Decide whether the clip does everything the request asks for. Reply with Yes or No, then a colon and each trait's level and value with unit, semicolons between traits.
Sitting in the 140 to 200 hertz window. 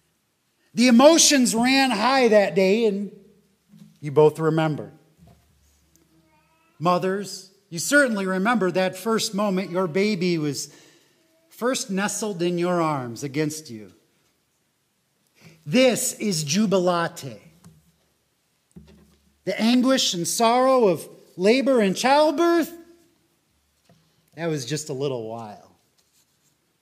Yes: medium, 185 Hz